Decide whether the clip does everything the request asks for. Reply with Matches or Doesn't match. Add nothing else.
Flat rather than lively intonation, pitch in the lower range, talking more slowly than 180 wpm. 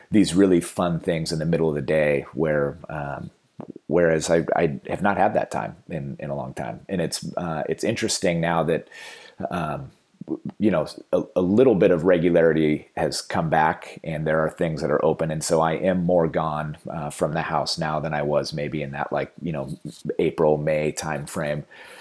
Doesn't match